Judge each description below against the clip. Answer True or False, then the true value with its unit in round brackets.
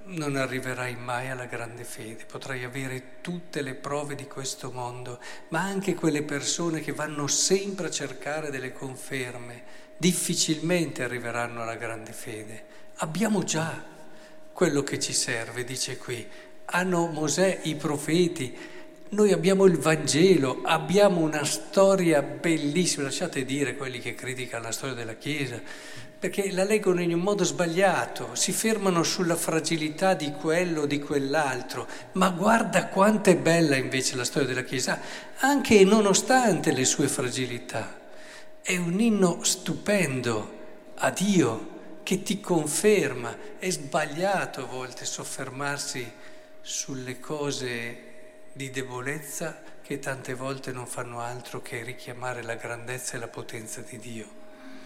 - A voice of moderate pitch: True (150 Hz)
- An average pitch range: False (6.0 semitones)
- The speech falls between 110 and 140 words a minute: True (135 wpm)